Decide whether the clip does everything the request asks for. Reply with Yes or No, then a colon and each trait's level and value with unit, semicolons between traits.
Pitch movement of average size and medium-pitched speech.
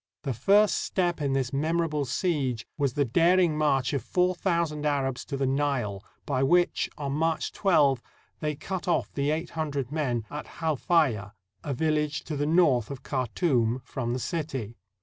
Yes: average, 3.7 semitones; medium, 145 Hz